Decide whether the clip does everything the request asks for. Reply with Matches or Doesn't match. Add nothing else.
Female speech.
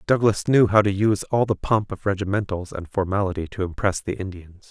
Doesn't match